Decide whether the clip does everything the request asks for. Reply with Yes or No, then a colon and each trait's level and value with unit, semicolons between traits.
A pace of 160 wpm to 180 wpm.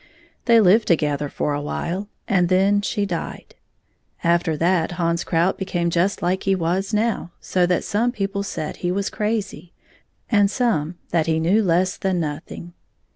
Yes: average, 165 wpm